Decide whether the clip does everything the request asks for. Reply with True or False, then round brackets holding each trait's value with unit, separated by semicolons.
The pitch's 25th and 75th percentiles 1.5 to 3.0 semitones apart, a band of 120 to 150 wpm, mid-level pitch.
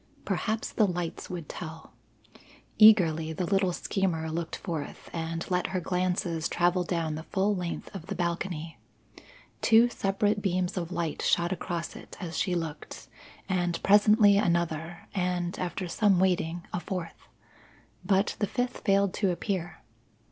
True (2.6 semitones; 145 wpm; 180 Hz)